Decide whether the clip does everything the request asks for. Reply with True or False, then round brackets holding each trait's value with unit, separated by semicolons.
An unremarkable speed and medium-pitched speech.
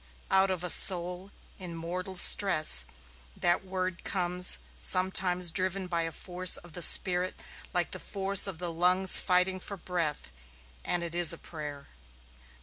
True (150 wpm; 180 Hz)